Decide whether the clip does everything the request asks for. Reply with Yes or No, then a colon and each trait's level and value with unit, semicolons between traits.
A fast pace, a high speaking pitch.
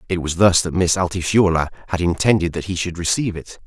No: fast, 215 wpm; very low, 90 Hz